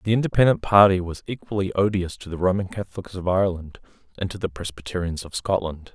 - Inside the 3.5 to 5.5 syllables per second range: No, 6.3 syllables/s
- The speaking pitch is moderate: No, very low, 95 Hz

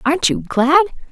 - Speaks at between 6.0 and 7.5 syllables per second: No, 5.4 syllables/s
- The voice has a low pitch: No, very high, 305 Hz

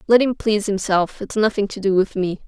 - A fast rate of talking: Yes, fast, 245 wpm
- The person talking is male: No, female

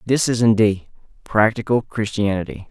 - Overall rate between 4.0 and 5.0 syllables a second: Yes, 4.9 syllables/s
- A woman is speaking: No, male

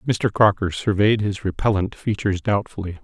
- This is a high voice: No, low, 105 Hz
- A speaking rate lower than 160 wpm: Yes, average, 140 wpm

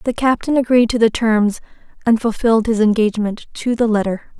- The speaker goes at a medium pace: Yes, average, 180 wpm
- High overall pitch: Yes, high, 225 Hz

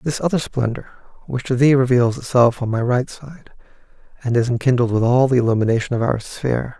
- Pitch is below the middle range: Yes, low, 125 Hz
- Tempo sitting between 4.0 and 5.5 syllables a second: No, 5.9 syllables/s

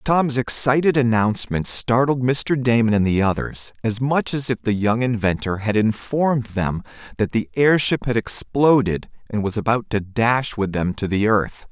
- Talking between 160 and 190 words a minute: Yes, average, 175 wpm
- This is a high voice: No, low, 115 Hz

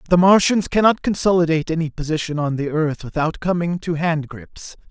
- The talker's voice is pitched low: No, medium, 165 Hz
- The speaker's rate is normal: Yes, average, 170 wpm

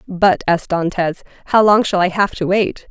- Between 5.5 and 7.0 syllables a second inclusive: No, 4.9 syllables/s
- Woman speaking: Yes, female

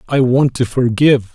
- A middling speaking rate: Yes, average, 180 wpm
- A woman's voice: No, male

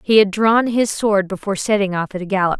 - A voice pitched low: No, high, 200 Hz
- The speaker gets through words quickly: Yes, fast, 255 wpm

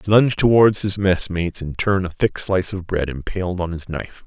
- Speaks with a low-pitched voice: Yes, very low, 95 Hz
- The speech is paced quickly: Yes, fast, 225 wpm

